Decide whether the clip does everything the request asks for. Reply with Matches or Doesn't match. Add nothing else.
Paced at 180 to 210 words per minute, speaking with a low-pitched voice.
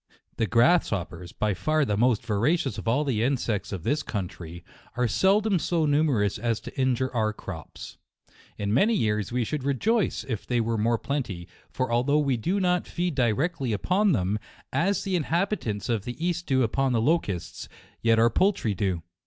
Matches